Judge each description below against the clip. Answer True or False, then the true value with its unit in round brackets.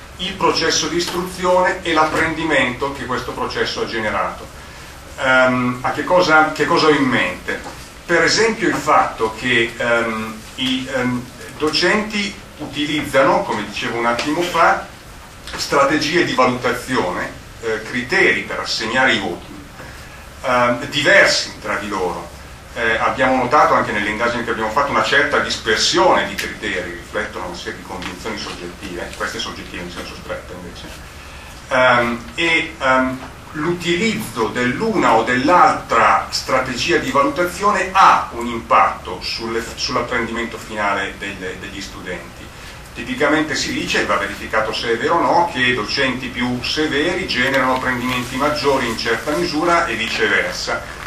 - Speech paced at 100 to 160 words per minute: True (135 wpm)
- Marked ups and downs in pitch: True (6.0 semitones)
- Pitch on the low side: True (125 Hz)